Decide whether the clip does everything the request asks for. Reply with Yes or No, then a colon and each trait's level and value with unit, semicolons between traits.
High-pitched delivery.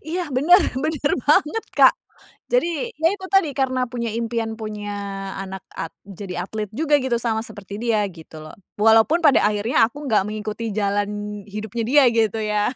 Yes: high, 225 Hz